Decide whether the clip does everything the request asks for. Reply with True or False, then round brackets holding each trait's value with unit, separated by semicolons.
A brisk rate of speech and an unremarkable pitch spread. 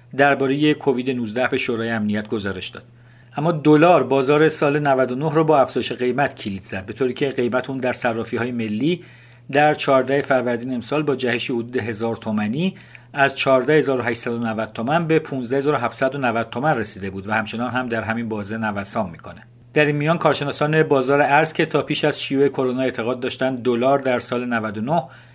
True (170 wpm; 3.4 semitones)